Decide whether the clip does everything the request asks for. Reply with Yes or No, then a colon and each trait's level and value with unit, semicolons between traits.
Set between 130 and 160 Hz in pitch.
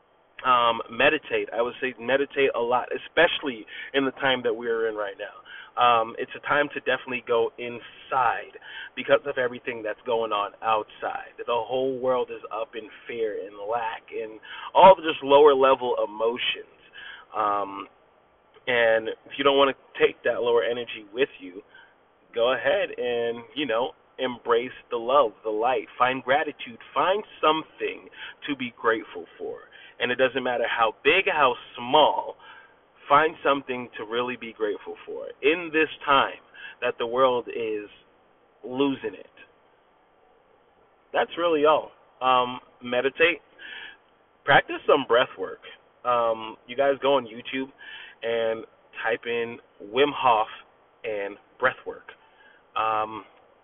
Yes: medium, 140 Hz